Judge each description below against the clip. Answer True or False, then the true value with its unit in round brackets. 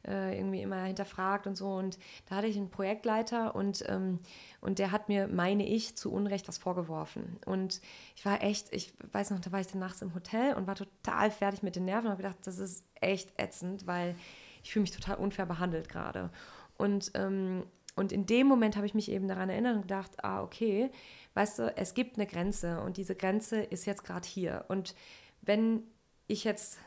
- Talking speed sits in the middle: False (205 wpm)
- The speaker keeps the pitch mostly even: True (1.8 semitones)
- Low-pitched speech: False (195 Hz)